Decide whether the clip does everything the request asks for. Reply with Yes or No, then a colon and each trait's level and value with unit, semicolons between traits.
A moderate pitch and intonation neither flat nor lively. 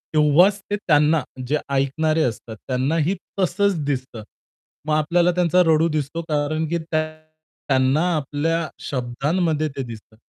Yes: medium, 155 Hz; average, 3.2 semitones